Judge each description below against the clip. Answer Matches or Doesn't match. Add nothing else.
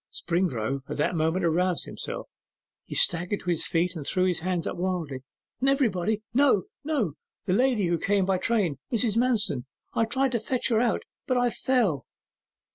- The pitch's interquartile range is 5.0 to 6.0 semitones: Matches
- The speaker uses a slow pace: Doesn't match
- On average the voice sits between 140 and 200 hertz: Matches